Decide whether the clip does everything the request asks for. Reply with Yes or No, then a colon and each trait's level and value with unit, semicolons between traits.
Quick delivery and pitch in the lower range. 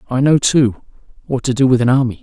Yes: fast, 245 wpm; low, 125 Hz